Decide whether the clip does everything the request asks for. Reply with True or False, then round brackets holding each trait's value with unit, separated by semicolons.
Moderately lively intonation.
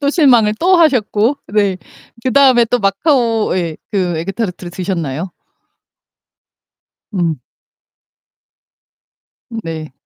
False (5.8 semitones)